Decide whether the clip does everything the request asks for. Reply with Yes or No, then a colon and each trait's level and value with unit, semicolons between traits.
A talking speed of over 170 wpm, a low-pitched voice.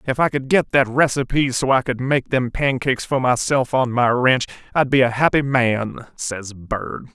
Yes: average, 200 wpm; low, 130 Hz